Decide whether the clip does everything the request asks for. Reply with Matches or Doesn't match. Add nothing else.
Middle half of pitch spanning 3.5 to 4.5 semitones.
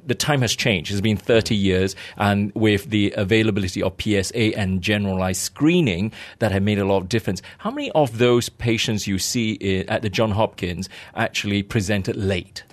Doesn't match